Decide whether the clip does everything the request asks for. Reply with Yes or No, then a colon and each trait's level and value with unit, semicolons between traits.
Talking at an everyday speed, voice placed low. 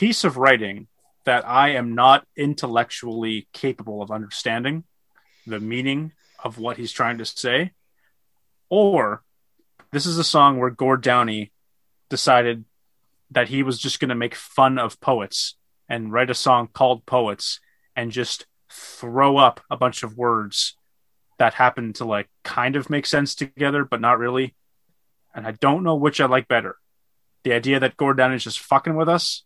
Yes: average, 165 wpm; low, 125 Hz